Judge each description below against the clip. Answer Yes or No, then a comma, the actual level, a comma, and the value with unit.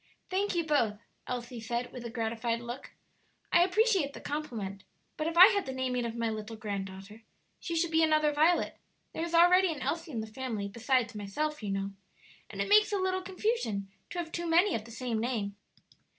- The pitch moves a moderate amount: No, wide, 7.3 semitones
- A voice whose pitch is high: Yes, very high, 255 Hz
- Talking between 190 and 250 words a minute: Yes, average, 200 wpm